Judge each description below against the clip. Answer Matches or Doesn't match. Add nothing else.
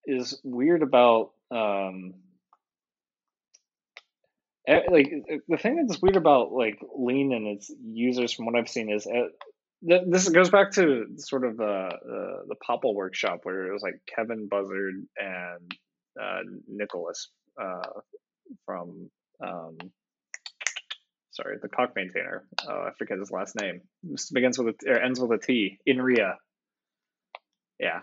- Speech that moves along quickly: Doesn't match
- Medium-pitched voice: Doesn't match